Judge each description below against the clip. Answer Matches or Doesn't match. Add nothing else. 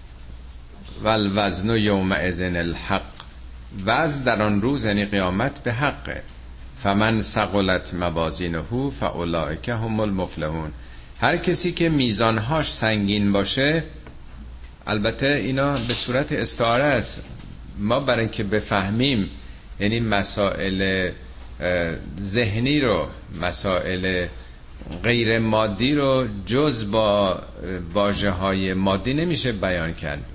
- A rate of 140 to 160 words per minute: Doesn't match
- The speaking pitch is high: Doesn't match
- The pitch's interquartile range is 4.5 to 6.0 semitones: Matches